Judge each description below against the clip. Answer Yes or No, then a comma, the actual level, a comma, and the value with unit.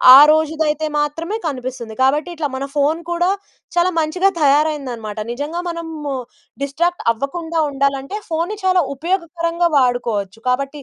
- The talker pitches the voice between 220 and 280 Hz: No, very high, 305 Hz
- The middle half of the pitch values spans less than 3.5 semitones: No, average, 3.8 semitones